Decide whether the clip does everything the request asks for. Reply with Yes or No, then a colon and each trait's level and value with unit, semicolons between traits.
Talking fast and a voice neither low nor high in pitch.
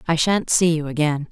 Yes: fast, 230 wpm; medium, 160 Hz